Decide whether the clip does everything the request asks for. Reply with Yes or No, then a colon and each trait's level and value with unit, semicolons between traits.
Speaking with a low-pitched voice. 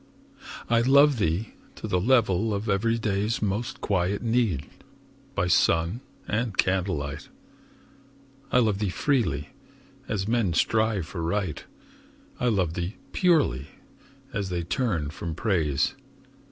Yes: low, 100 Hz